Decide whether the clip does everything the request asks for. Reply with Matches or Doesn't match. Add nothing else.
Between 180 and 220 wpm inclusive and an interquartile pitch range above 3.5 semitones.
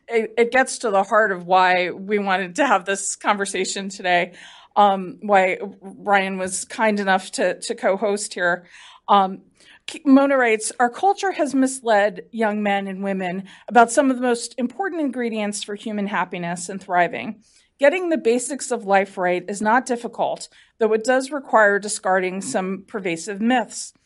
Doesn't match